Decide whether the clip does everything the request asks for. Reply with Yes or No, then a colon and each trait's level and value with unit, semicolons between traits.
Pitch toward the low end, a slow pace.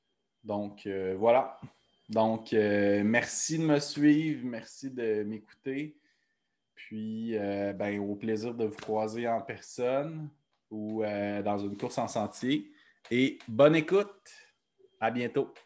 Yes: low, 115 Hz; slow, 130 wpm